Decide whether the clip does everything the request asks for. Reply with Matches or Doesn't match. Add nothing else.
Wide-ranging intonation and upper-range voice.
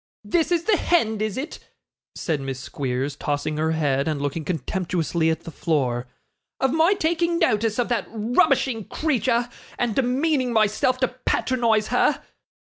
Matches